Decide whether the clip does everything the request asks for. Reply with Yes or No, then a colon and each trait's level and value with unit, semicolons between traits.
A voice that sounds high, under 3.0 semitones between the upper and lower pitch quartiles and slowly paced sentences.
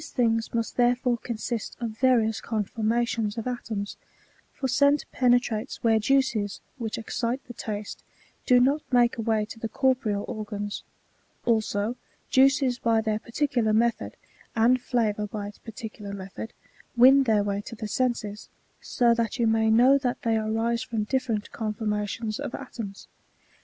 No: high, 230 Hz; narrow, 2.5 semitones; average, 150 wpm